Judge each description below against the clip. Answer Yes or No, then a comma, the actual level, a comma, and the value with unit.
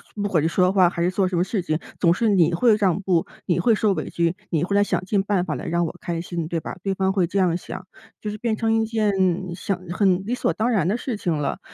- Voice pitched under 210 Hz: Yes, high, 190 Hz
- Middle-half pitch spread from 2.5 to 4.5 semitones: Yes, average, 3.3 semitones